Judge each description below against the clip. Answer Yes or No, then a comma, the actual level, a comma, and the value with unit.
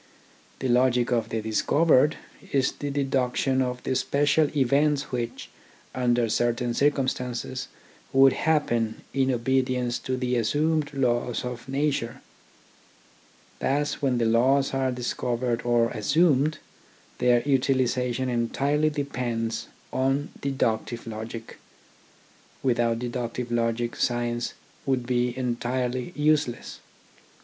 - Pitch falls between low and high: No, low, 125 Hz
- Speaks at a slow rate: Yes, slow, 110 wpm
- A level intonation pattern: Yes, narrow, 2.3 semitones